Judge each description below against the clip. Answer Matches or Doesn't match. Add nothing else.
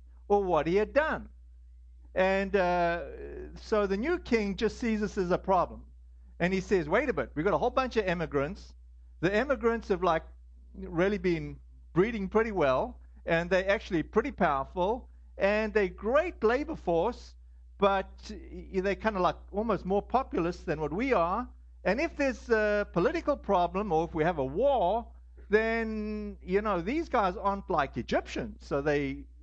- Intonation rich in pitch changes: Matches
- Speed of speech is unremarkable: Matches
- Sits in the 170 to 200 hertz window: Matches